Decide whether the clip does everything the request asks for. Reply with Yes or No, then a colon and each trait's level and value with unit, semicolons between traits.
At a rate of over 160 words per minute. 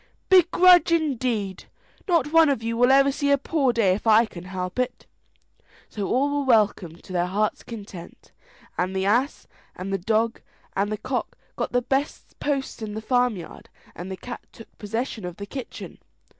Yes: average, 180 wpm